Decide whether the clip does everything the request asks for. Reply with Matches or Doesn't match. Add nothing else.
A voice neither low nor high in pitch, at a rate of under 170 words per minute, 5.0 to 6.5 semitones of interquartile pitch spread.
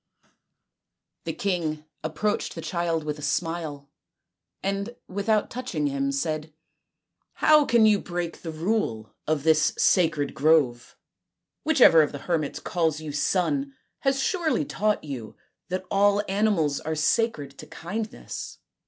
Matches